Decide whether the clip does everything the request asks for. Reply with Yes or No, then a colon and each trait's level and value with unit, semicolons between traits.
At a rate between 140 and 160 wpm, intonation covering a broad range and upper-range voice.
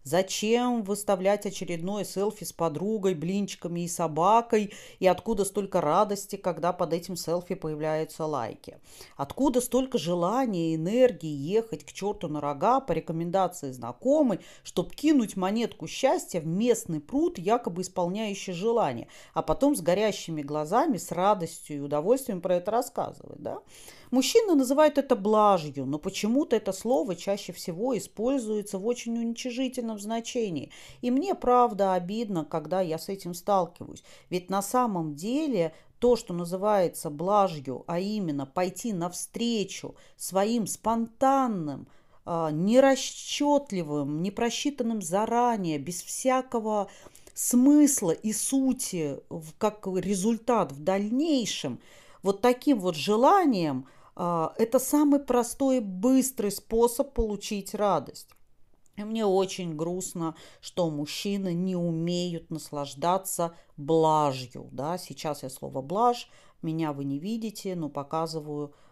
No: average, 120 wpm; wide, 5.7 semitones; high, 195 Hz